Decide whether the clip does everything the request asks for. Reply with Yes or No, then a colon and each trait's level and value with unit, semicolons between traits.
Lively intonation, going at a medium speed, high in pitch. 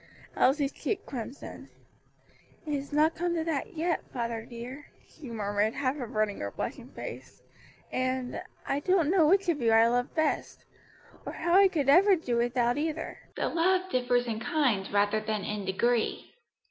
Yes: wide, 5.7 semitones; average, 165 wpm; very high, 260 Hz